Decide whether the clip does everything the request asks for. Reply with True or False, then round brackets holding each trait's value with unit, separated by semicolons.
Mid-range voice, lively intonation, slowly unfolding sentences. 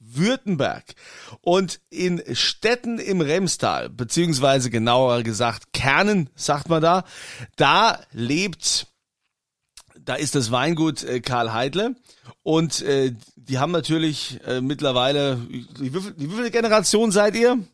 True (150 Hz; 6.6 semitones; 115 wpm)